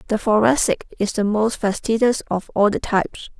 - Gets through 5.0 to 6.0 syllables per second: Yes, 5.1 syllables/s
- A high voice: Yes, high, 215 Hz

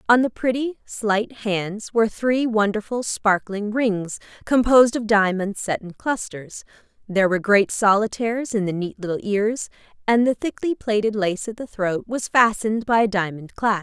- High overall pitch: Yes, high, 215 Hz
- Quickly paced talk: No, average, 170 wpm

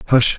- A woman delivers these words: No, male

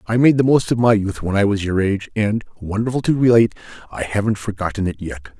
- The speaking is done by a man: Yes, male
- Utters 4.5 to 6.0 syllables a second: No, 6.2 syllables/s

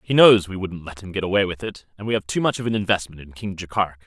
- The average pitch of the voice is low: Yes, very low, 95 Hz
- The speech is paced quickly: Yes, fast, 295 wpm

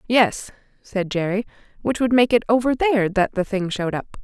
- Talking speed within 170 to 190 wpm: No, average, 200 wpm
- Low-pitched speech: No, high, 215 Hz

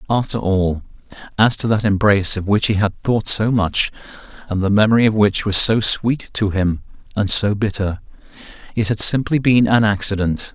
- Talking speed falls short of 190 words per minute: Yes, average, 175 wpm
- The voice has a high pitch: No, low, 105 Hz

